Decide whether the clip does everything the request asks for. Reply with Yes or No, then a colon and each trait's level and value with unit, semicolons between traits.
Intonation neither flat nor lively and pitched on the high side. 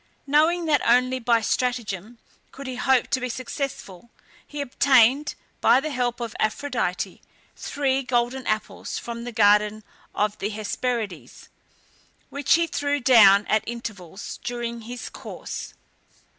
Yes: average, 3.6 semitones; high, 245 Hz